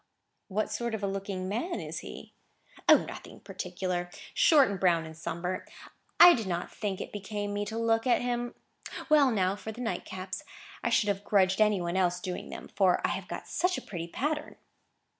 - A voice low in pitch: No, high, 200 Hz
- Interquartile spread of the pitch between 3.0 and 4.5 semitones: Yes, average, 3.7 semitones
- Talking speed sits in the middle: Yes, average, 195 wpm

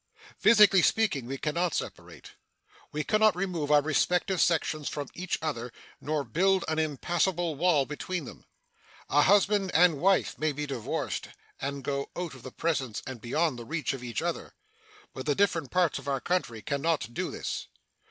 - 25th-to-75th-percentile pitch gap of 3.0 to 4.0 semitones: No, average, 4.5 semitones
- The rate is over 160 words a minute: Yes, average, 180 wpm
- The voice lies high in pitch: No, medium, 155 Hz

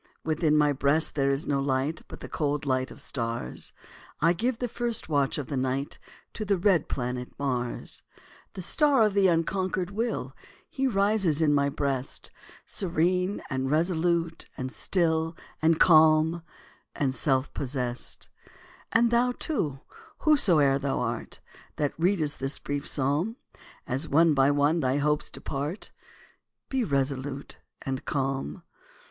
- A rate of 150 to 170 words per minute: No, average, 140 wpm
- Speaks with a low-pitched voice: No, medium, 150 Hz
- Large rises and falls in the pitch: No, average, 4.8 semitones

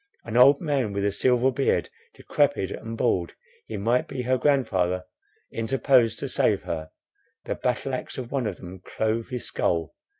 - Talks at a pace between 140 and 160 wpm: No, average, 170 wpm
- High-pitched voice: No, low, 120 Hz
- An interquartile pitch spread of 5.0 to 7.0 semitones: No, average, 4.3 semitones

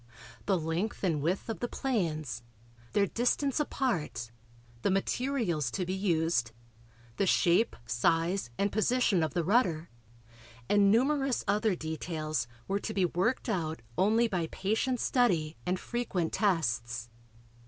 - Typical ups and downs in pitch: No, wide, 5.7 semitones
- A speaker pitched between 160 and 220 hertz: Yes, medium, 185 Hz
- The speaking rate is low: Yes, slow, 130 wpm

